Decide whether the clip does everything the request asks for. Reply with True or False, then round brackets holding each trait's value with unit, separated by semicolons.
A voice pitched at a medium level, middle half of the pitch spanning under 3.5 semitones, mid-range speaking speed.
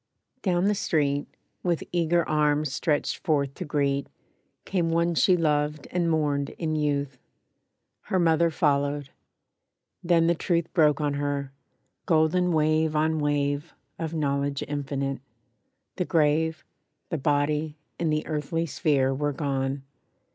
False (150 Hz; 2.5 semitones; 130 wpm)